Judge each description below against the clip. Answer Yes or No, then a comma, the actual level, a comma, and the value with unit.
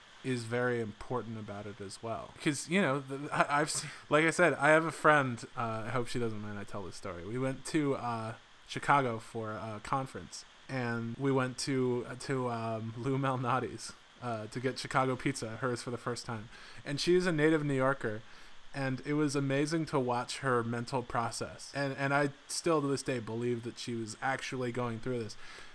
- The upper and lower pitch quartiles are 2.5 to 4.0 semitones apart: Yes, average, 3.0 semitones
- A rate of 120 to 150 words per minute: No, average, 200 wpm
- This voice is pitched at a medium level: No, low, 125 Hz